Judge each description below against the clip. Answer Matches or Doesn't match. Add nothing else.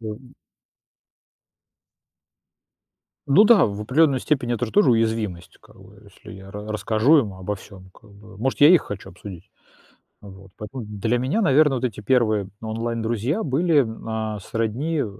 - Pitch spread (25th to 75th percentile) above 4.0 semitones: Matches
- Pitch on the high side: Doesn't match